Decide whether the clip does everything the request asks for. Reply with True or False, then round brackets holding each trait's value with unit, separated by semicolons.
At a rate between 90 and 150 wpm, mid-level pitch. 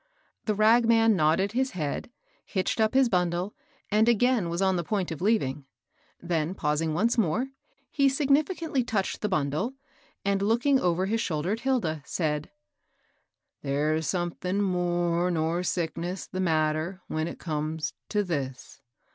True (145 wpm; 180 Hz)